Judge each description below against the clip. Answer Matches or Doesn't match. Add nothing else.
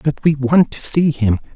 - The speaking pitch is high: Doesn't match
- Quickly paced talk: Matches